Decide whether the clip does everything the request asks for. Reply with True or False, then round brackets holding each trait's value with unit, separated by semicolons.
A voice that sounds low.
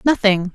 False (210 Hz)